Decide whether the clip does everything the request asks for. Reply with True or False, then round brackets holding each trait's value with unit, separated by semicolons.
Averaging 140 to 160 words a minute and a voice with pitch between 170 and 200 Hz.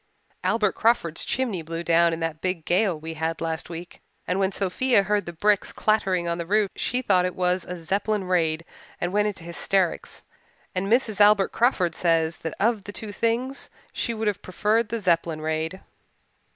False (185 wpm; 185 Hz)